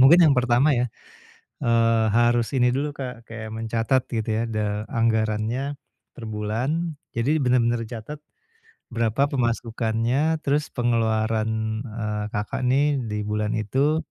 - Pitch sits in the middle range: No, low, 115 Hz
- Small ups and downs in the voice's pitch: No, average, 3.3 semitones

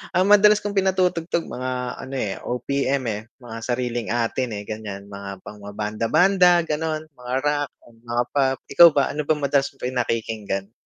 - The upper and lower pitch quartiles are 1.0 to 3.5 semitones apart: No, wide, 5.5 semitones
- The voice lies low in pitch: Yes, low, 130 Hz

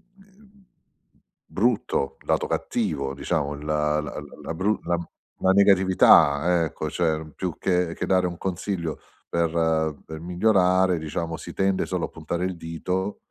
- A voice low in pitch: Yes, very low, 85 Hz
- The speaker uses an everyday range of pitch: Yes, average, 3.1 semitones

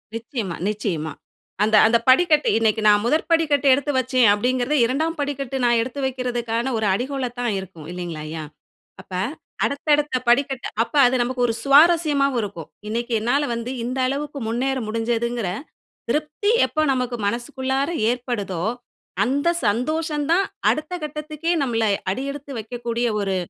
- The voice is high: Yes, very high, 250 Hz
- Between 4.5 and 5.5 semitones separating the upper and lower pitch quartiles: No, average, 4.0 semitones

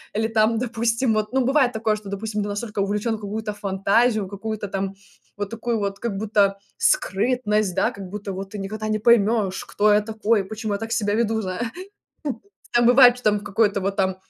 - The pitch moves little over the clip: Yes, narrow, 2.1 semitones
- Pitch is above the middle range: Yes, high, 215 Hz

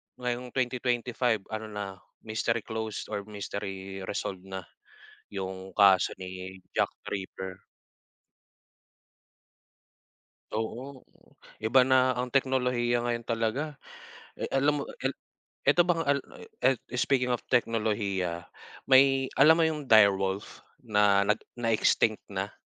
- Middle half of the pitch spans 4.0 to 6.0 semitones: Yes, average, 4.4 semitones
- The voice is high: No, low, 115 Hz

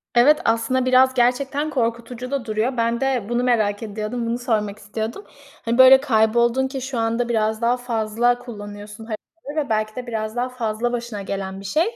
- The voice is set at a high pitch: Yes, high, 235 Hz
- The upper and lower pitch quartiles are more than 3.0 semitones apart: No, average, 2.7 semitones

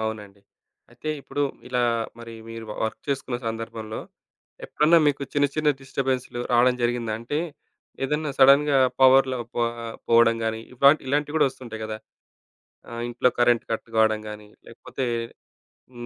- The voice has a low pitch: Yes, low, 120 Hz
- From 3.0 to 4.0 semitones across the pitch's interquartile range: Yes, average, 3.4 semitones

